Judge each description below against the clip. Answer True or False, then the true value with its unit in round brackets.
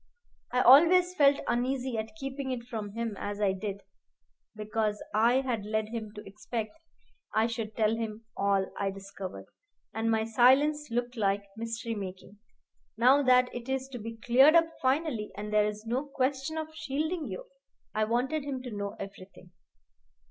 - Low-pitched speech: False (230 Hz)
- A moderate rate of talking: True (165 wpm)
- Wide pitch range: False (4.0 semitones)